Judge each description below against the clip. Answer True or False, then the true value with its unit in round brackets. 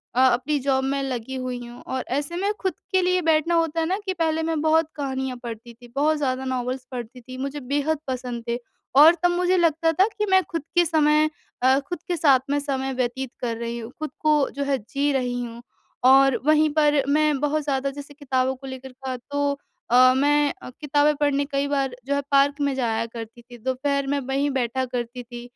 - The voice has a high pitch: True (275 Hz)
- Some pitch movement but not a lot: True (3.0 semitones)